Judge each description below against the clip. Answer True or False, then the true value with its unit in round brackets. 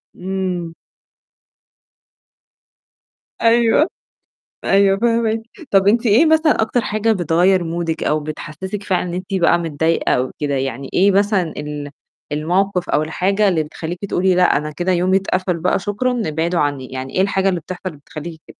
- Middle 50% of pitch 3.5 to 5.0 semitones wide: True (3.8 semitones)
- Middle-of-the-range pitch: True (180 Hz)